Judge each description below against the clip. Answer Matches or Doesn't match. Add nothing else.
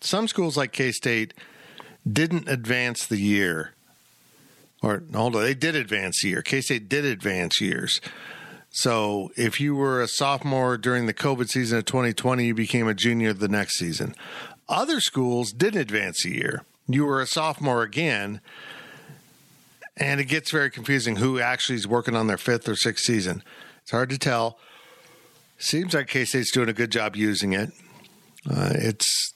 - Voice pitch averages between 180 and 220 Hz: Doesn't match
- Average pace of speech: Matches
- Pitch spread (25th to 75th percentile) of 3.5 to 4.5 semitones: Matches